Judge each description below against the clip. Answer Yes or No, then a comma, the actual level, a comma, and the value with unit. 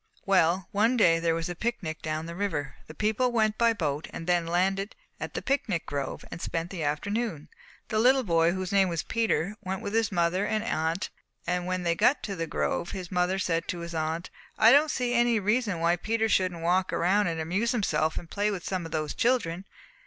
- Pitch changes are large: No, average, 4.4 semitones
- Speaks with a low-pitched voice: No, medium, 185 Hz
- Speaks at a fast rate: Yes, fast, 215 wpm